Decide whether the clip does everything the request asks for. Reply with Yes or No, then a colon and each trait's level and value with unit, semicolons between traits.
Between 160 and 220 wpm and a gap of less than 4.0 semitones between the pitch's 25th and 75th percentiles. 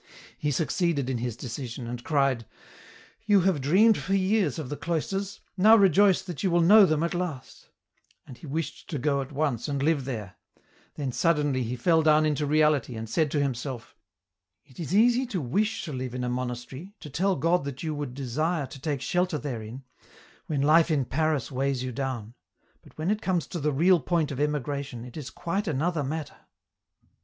No: average, 200 wpm; average, 4.8 semitones